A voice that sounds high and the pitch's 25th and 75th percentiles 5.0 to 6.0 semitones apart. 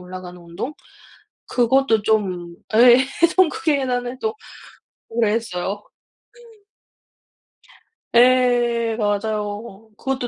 No: high, 225 Hz; average, 3.4 semitones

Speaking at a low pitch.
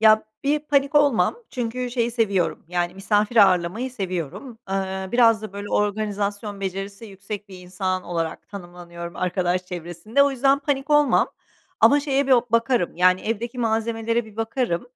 No: high, 215 Hz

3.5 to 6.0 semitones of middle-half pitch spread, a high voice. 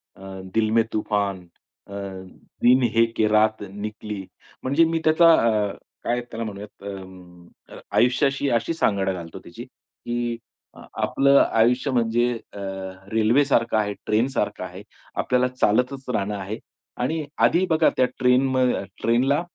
No: average, 3.8 semitones; low, 115 Hz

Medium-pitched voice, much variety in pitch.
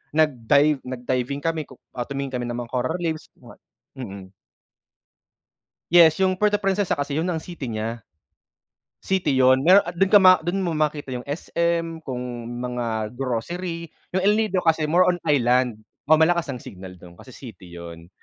Yes: medium, 145 Hz; wide, 5.8 semitones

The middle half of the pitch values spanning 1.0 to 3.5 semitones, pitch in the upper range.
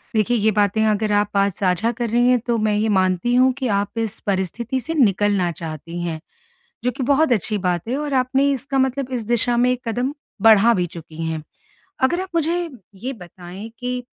No: average, 4.4 semitones; high, 225 Hz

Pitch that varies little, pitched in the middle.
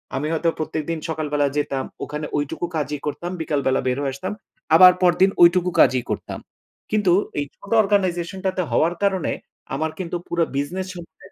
No: average, 3.8 semitones; medium, 165 Hz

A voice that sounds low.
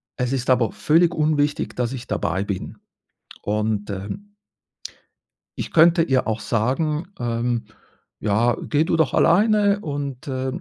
Yes: low, 130 Hz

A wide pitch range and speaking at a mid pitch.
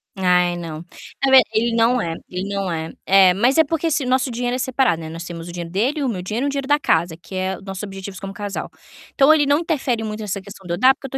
No: wide, 6.6 semitones; high, 205 Hz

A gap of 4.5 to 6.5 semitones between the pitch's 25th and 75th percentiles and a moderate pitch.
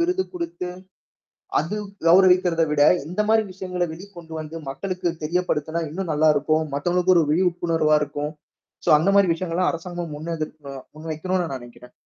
No: average, 2.9 semitones; medium, 170 Hz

